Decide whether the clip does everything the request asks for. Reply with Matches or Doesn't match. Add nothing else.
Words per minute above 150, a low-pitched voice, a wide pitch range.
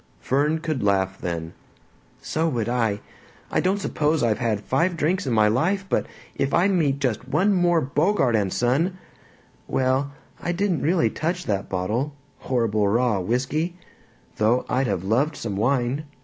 Matches